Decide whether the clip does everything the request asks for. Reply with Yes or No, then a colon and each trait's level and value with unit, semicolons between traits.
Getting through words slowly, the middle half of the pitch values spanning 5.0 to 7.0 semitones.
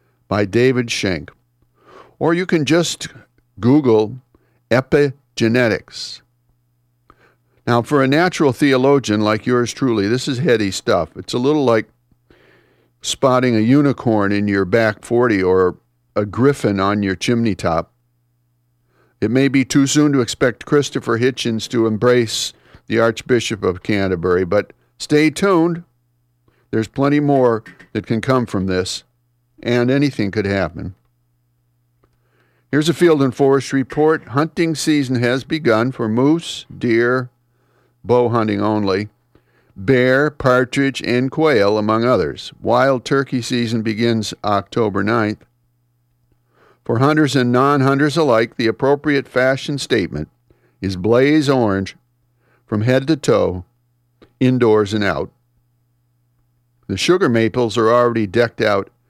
Yes: slow, 125 wpm; average, 5.3 semitones